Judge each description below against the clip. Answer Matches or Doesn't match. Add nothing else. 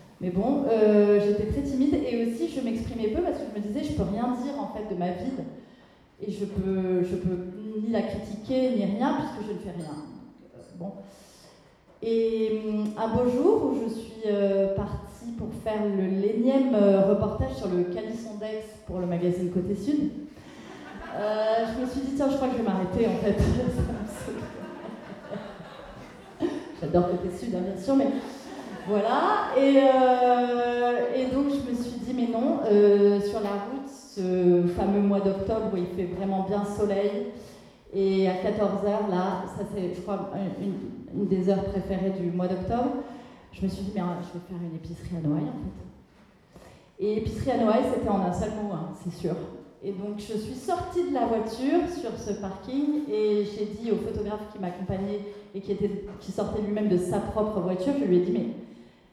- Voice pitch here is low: Doesn't match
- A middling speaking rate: Matches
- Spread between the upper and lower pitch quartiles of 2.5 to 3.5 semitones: Doesn't match